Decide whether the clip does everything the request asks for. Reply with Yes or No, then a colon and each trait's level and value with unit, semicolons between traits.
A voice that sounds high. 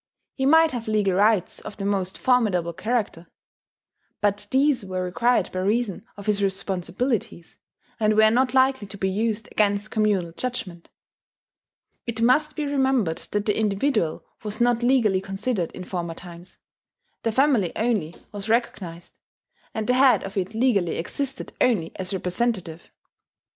Yes: high, 210 Hz